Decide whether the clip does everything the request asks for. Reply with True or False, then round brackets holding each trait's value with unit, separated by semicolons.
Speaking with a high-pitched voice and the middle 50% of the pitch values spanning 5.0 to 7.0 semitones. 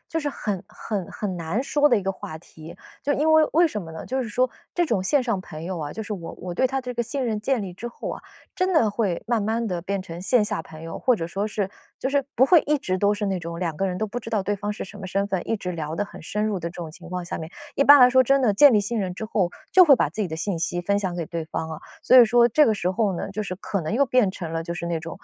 True (205 Hz; 5.5 semitones)